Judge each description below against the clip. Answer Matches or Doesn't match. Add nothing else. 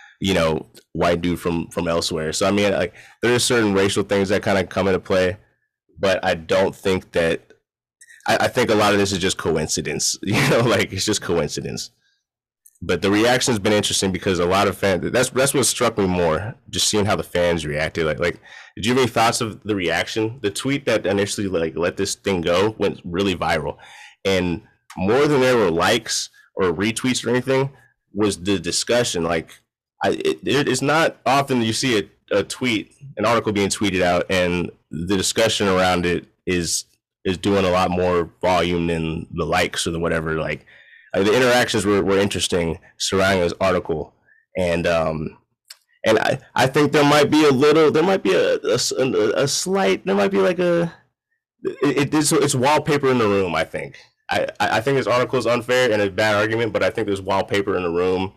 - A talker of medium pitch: Doesn't match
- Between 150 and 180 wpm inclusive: Doesn't match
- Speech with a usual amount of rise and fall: Doesn't match